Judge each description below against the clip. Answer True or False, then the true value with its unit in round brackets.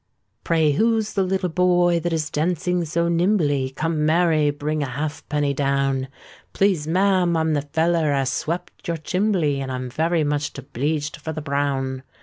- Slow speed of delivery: False (160 wpm)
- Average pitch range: True (3.3 semitones)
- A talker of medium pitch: True (155 Hz)